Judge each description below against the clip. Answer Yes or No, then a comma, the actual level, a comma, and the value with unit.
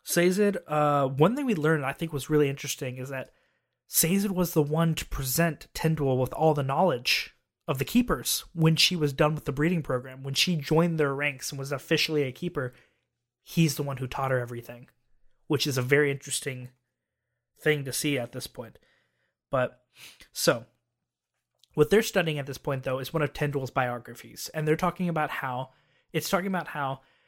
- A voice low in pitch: No, medium, 145 Hz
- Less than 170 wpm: No, average, 190 wpm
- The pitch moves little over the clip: No, average, 3.5 semitones